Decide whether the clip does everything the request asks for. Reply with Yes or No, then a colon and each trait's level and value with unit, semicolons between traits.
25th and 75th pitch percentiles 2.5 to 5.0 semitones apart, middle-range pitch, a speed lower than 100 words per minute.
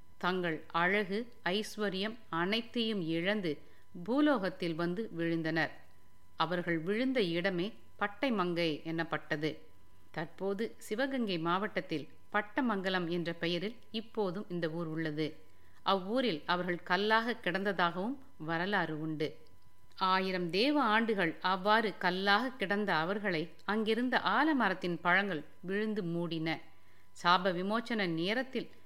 Yes: average, 4.4 semitones; medium, 180 Hz; average, 90 wpm